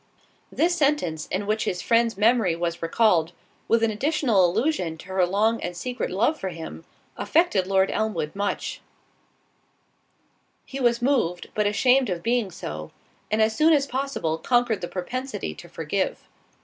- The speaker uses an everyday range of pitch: No, wide, 5.9 semitones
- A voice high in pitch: Yes, high, 215 Hz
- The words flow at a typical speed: Yes, average, 150 wpm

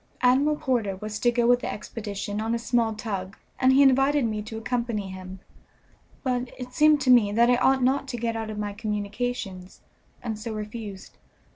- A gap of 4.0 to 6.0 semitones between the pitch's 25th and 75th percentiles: No, average, 3.1 semitones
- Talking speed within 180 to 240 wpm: Yes, average, 190 wpm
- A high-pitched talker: Yes, high, 230 Hz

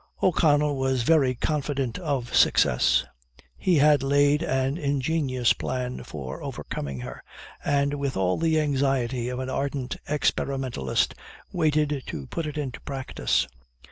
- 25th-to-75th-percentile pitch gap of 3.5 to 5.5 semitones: No, average, 2.8 semitones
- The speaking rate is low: Yes, slow, 130 wpm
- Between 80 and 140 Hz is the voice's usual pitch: Yes, low, 135 Hz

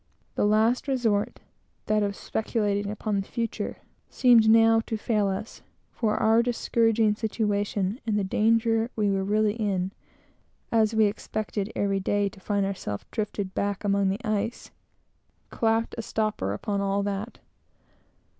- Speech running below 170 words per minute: Yes, average, 145 wpm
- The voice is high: Yes, high, 210 Hz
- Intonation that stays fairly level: Yes, narrow, 1.9 semitones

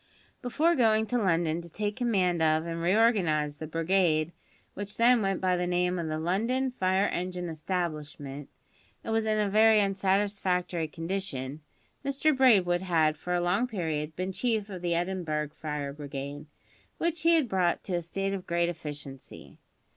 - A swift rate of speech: No, average, 165 wpm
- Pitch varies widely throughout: No, average, 4.5 semitones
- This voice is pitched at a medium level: Yes, medium, 180 Hz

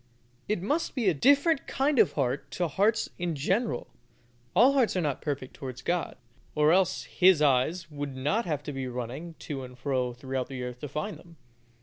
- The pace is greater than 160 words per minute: Yes, average, 195 wpm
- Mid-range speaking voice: Yes, medium, 150 Hz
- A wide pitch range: Yes, wide, 6.3 semitones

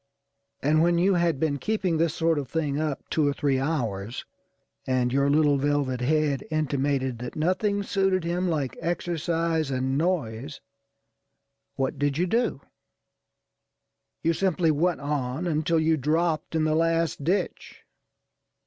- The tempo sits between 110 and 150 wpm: Yes, average, 140 wpm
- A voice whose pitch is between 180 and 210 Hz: No, medium, 155 Hz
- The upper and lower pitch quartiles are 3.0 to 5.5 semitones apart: Yes, average, 3.3 semitones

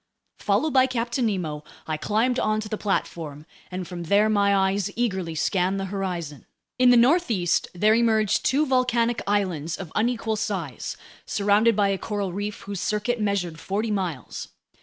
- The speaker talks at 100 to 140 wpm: No, average, 160 wpm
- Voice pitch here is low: No, high, 205 Hz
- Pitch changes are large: No, average, 3.9 semitones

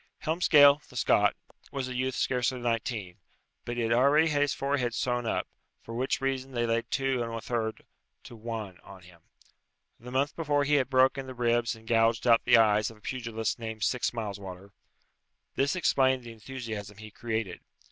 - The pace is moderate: Yes, average, 175 wpm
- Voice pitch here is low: Yes, low, 120 Hz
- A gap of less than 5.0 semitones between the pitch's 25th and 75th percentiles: Yes, average, 2.9 semitones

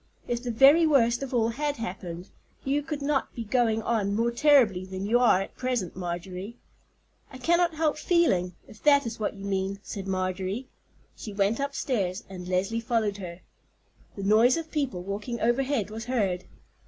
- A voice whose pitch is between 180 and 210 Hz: No, high, 225 Hz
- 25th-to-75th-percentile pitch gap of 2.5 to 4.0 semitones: No, wide, 5.4 semitones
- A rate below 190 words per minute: Yes, average, 175 wpm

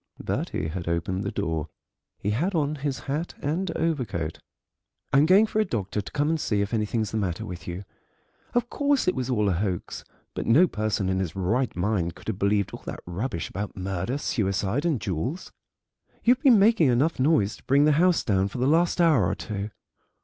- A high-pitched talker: No, low, 110 Hz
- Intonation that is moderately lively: No, wide, 8.1 semitones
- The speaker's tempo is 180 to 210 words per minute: Yes, fast, 205 wpm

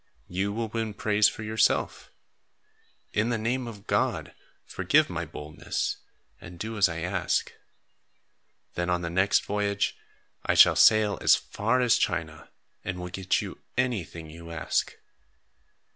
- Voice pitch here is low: Yes, low, 100 Hz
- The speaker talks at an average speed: Yes, average, 145 wpm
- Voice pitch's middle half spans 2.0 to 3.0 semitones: No, average, 3.9 semitones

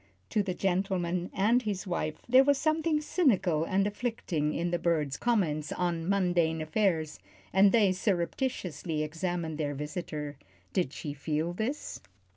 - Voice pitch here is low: No, medium, 175 Hz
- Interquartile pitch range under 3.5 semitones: No, average, 4.7 semitones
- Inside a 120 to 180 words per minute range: Yes, average, 140 wpm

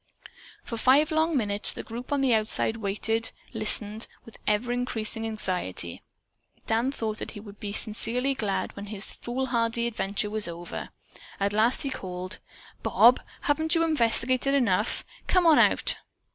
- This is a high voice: Yes, high, 225 Hz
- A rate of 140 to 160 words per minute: Yes, average, 155 wpm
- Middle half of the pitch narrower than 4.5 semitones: Yes, average, 3.7 semitones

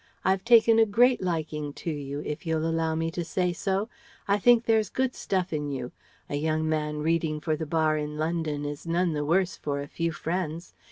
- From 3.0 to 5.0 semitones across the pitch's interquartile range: Yes, average, 3.6 semitones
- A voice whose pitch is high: No, medium, 165 Hz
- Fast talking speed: Yes, fast, 210 wpm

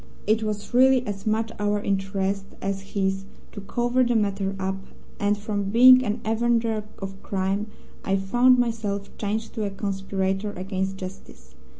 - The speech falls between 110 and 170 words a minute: Yes, average, 155 wpm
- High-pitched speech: Yes, high, 205 Hz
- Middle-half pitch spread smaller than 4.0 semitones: Yes, narrow, 2.5 semitones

